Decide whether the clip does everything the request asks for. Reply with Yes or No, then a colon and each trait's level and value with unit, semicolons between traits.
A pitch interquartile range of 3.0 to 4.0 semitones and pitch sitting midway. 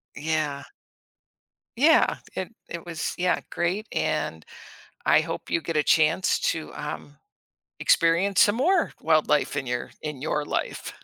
Yes: average, 3.5 semitones; medium, 160 Hz